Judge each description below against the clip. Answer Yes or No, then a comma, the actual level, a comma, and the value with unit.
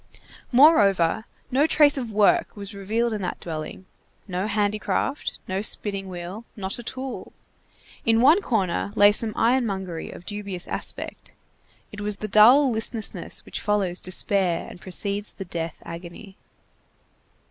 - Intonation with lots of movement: No, average, 3.3 semitones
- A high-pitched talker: Yes, high, 205 Hz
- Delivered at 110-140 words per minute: Yes, slow, 135 wpm